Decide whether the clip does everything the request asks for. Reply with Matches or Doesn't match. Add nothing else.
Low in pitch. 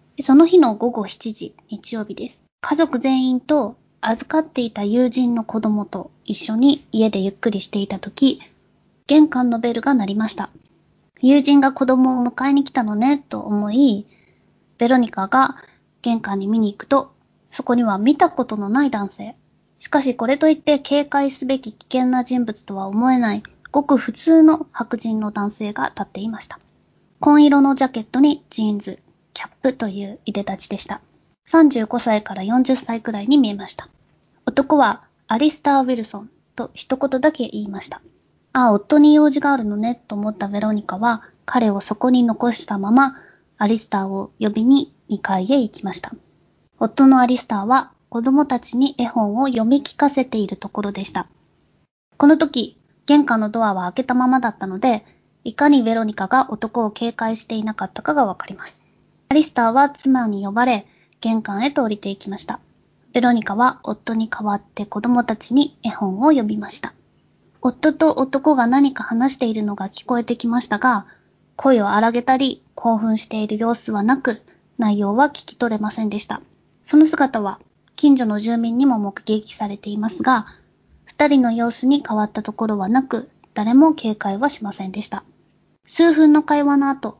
Doesn't match